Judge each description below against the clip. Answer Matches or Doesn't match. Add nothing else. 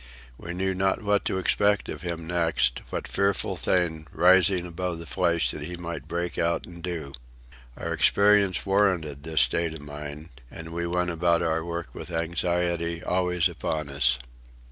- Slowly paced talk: Doesn't match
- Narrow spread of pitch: Matches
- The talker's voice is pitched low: Matches